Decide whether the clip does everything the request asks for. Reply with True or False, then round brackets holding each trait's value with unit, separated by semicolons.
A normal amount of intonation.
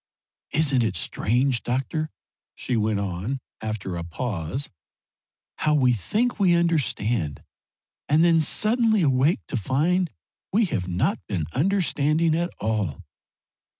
False (7.8 semitones)